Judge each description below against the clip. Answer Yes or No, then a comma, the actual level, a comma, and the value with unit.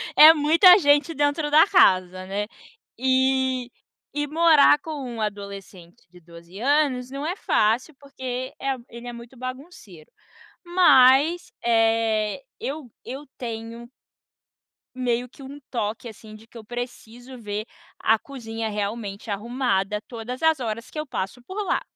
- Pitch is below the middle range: No, high, 245 Hz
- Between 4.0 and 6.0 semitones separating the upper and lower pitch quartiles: Yes, average, 4.7 semitones